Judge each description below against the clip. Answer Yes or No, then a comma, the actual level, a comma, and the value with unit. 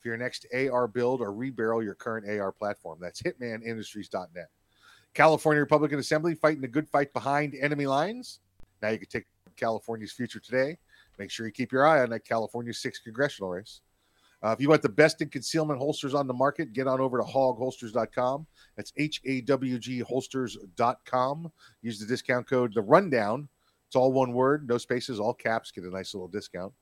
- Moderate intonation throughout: Yes, average, 3.8 semitones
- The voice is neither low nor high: No, low, 125 Hz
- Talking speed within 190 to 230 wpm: No, average, 180 wpm